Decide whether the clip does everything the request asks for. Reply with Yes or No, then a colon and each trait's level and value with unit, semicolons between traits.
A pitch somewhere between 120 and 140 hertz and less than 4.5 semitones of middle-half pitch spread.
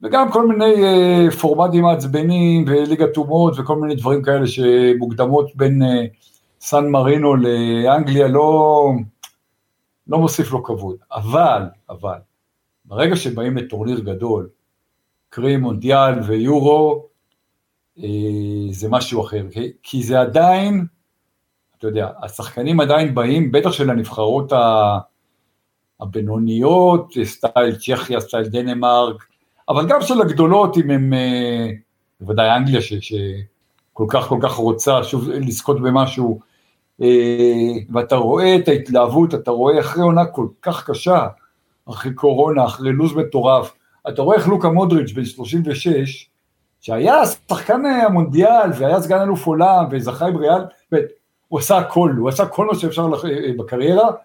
No: low, 135 Hz; wide, 5.5 semitones